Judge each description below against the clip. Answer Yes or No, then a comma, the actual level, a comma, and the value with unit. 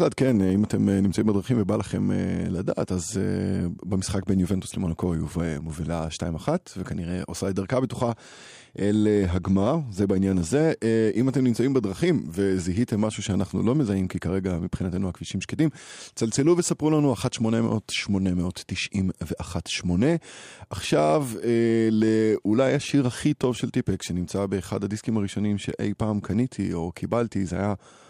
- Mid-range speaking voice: No, low, 100 Hz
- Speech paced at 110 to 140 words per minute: Yes, average, 135 wpm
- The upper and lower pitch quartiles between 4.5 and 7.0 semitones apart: No, average, 3.9 semitones